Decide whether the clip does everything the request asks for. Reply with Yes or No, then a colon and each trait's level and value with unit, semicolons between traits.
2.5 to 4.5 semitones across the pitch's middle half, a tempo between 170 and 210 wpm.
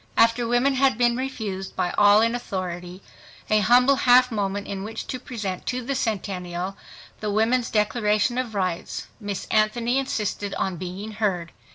No: average, 3.9 semitones; average, 160 wpm